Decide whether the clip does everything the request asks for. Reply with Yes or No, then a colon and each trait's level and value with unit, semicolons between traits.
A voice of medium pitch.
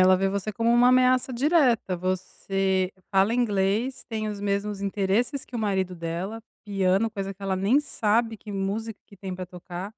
No: high, 200 Hz